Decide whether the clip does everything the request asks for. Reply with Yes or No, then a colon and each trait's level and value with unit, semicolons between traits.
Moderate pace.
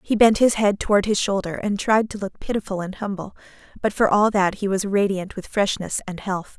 No: fast, 230 wpm